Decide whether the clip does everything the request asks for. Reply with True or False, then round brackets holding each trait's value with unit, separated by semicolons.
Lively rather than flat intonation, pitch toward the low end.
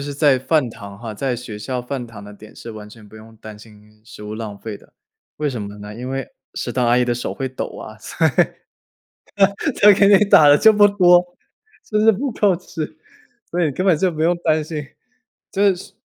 True (8.0 semitones; 130 Hz)